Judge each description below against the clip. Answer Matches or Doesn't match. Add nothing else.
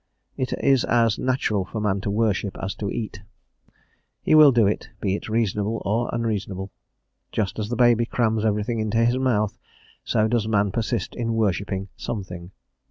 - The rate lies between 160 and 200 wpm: Matches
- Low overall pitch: Matches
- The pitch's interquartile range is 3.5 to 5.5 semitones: Doesn't match